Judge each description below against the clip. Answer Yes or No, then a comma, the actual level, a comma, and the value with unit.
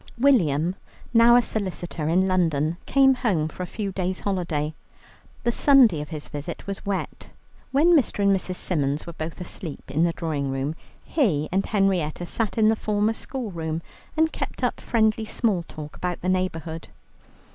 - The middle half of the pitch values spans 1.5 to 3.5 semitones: No, wide, 5.4 semitones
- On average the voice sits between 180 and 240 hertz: Yes, medium, 185 Hz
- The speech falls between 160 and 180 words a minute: Yes, average, 170 wpm